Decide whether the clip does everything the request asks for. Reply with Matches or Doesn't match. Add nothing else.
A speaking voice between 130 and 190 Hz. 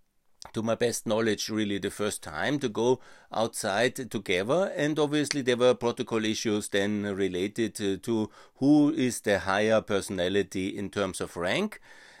Doesn't match